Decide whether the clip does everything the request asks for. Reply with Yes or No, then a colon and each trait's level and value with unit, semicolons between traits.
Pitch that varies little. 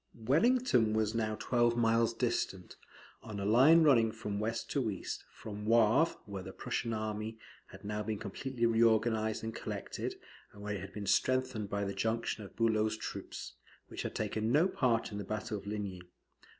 Yes: narrow, 2.0 semitones